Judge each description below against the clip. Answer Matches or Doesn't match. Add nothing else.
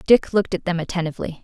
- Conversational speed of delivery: Doesn't match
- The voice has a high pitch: Doesn't match